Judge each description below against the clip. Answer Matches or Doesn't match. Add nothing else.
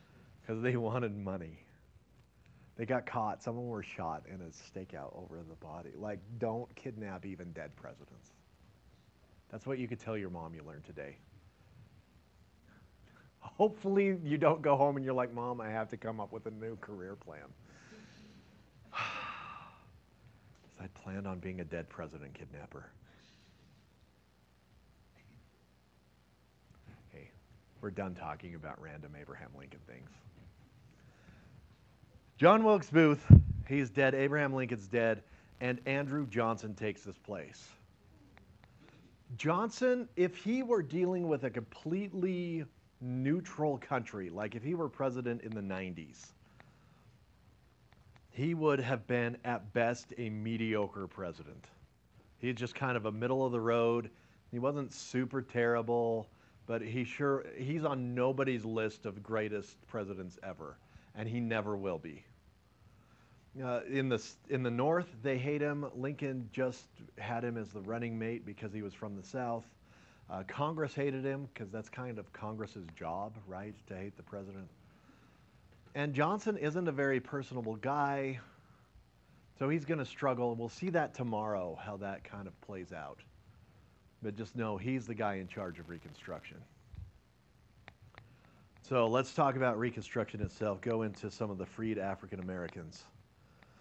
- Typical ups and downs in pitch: Matches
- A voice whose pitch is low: Matches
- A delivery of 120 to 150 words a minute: Matches